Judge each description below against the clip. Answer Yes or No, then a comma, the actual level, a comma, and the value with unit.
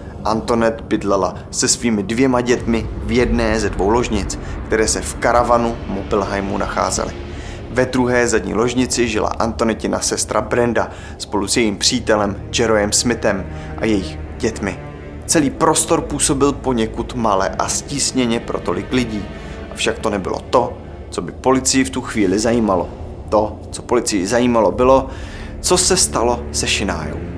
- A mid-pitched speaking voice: No, low, 110 Hz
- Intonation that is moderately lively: Yes, average, 4.6 semitones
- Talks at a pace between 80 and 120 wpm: No, average, 140 wpm